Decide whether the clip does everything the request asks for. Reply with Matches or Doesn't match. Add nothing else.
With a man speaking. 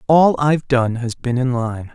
Matches